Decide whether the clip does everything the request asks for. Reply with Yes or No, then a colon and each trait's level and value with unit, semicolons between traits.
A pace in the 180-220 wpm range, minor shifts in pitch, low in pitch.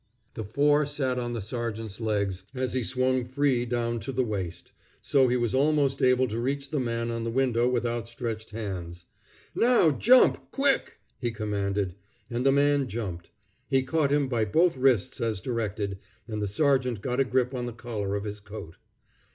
No: average, 185 wpm; average, 3.6 semitones; low, 120 Hz